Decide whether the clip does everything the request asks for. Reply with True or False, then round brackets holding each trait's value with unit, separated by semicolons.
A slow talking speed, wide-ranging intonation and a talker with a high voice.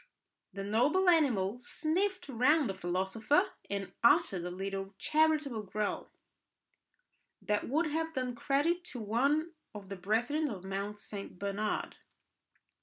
True (125 wpm; 7.5 semitones; 230 Hz)